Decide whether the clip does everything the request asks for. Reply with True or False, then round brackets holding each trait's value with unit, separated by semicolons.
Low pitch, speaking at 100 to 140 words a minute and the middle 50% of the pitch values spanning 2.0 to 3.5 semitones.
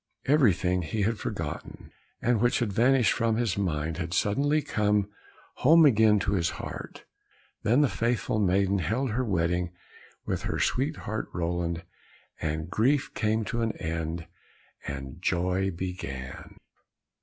False (100 Hz; 135 wpm; 5.2 semitones)